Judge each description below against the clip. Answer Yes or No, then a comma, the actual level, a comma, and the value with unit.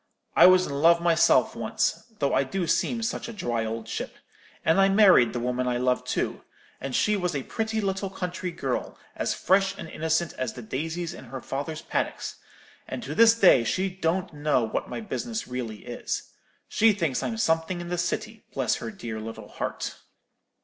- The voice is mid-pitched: Yes, medium, 165 Hz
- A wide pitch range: Yes, wide, 7.2 semitones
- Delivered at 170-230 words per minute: Yes, average, 190 wpm